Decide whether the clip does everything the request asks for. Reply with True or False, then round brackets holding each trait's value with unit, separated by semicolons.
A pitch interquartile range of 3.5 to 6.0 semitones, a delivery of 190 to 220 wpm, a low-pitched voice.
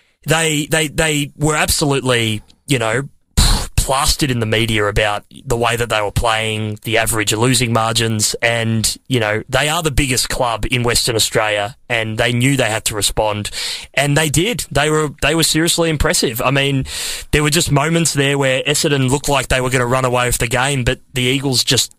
True (4.3 semitones; 200 wpm; 125 Hz)